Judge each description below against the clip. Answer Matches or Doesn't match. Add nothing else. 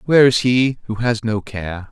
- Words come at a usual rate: Doesn't match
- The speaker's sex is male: Matches